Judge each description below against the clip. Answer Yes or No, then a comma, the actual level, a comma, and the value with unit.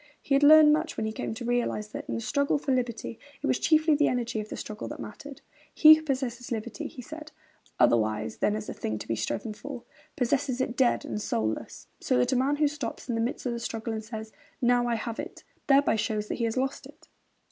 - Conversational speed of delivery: No, fast, 240 wpm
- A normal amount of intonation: Yes, average, 4.2 semitones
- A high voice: Yes, high, 240 Hz